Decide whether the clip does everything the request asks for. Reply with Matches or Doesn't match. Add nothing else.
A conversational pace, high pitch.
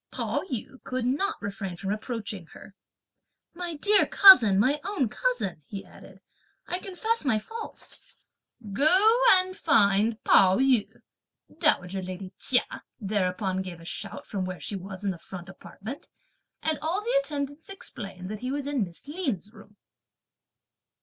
Matches